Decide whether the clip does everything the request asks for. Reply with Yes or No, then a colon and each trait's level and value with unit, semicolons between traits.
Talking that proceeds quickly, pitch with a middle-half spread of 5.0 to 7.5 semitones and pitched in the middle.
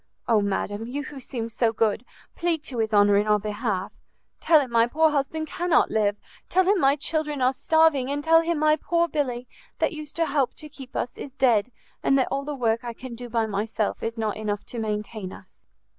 No: fast, 220 wpm; wide, 5.5 semitones; very high, 250 Hz